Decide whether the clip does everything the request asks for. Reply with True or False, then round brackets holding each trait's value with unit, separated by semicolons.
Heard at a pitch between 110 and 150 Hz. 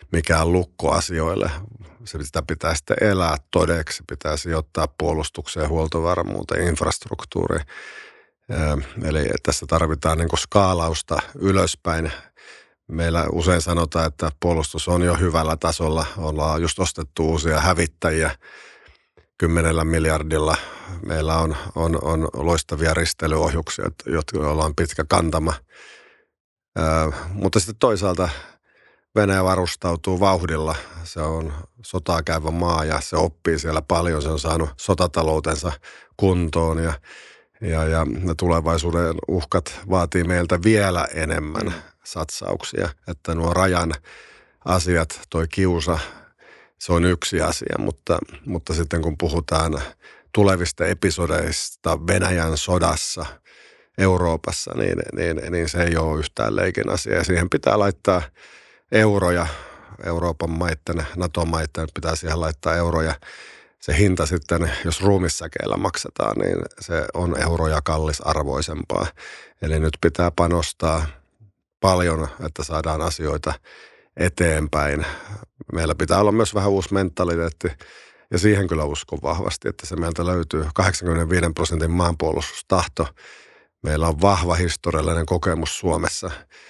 False (85 Hz)